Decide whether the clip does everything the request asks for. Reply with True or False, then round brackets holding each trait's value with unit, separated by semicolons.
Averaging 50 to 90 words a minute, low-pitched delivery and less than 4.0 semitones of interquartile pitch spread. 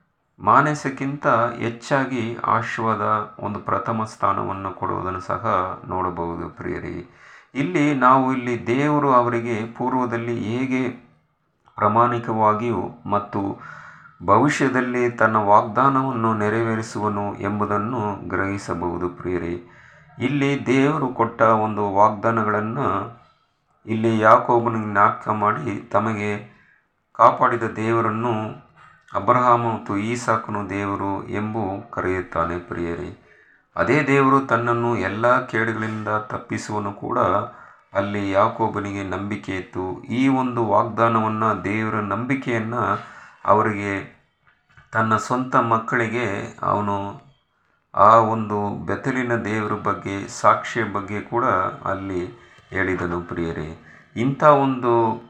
True (85 wpm; 110 Hz; 3.1 semitones)